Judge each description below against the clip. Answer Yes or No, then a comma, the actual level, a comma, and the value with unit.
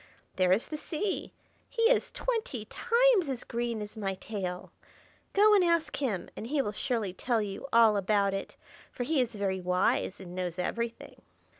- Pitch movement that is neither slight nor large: No, wide, 7.8 semitones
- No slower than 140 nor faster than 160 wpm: No, average, 175 wpm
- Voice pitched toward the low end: No, high, 230 Hz